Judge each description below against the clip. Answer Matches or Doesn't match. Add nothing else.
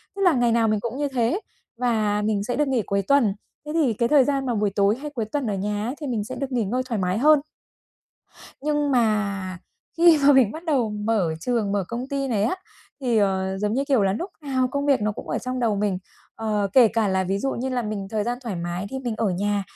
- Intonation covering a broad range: Doesn't match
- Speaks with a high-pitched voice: Matches